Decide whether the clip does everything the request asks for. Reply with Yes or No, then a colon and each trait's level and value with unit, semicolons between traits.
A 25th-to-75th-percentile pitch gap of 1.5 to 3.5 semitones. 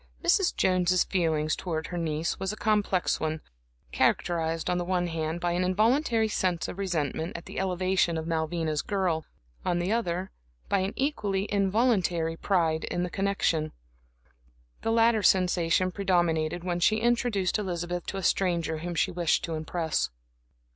Yes: average, 3.0 semitones